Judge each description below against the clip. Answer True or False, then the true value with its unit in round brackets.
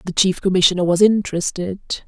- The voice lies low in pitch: False (185 Hz)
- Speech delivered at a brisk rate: False (145 wpm)